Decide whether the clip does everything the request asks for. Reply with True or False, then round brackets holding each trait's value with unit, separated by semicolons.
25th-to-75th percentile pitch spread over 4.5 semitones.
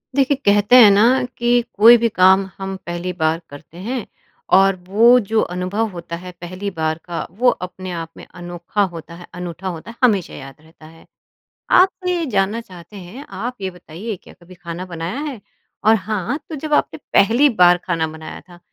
True (5.0 semitones)